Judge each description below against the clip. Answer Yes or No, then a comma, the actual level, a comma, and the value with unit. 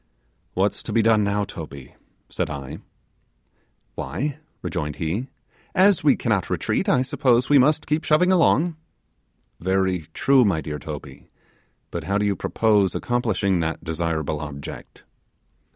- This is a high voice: No, low, 100 Hz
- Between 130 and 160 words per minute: Yes, slow, 135 wpm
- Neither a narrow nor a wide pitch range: No, wide, 8.3 semitones